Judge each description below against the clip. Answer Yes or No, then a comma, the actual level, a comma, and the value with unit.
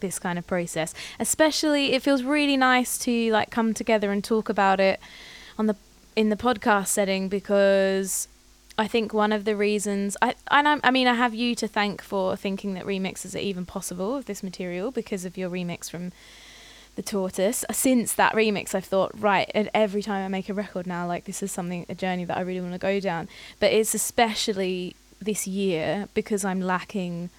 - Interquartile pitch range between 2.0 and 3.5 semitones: Yes, average, 2.8 semitones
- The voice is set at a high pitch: Yes, high, 200 Hz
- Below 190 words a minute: No, fast, 205 wpm